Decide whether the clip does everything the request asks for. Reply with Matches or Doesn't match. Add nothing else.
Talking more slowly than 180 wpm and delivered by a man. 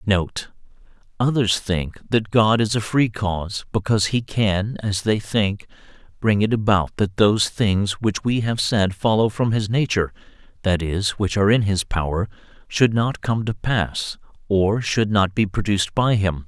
Matches